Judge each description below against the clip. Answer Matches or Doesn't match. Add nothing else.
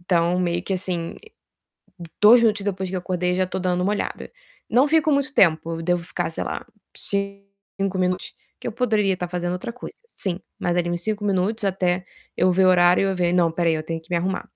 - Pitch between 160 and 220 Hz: Matches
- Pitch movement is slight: Matches